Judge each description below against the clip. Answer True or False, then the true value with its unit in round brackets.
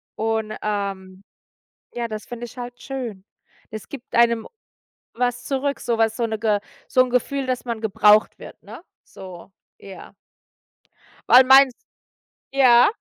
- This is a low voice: False (230 Hz)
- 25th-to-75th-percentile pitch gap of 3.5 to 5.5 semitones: False (2.8 semitones)